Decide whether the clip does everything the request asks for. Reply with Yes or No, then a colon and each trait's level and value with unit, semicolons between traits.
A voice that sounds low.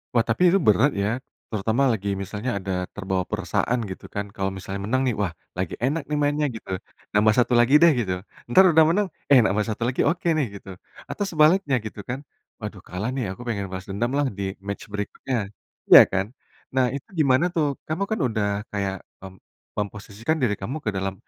Yes: low, 110 Hz